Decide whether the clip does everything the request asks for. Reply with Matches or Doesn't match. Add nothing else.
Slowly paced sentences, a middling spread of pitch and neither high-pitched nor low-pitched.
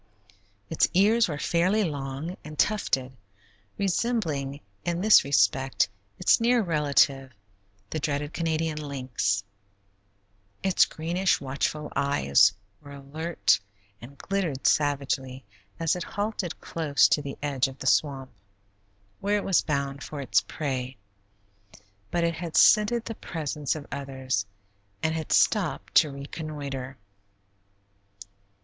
Matches